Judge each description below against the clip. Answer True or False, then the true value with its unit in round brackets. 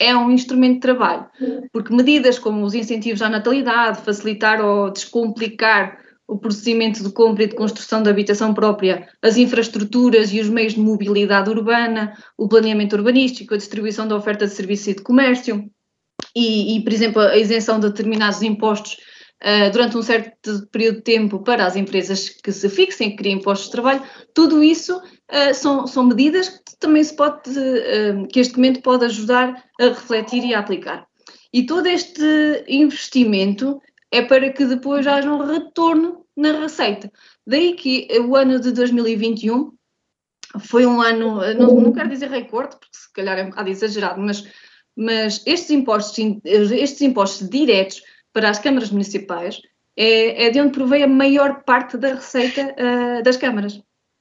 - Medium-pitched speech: False (230 Hz)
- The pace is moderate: True (165 wpm)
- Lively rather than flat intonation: False (3.4 semitones)